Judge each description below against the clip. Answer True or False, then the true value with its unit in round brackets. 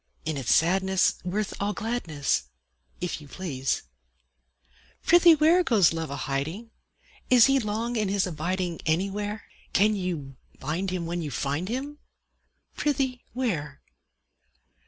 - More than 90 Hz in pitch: True (190 Hz)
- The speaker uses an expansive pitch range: True (6.3 semitones)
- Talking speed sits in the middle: False (130 wpm)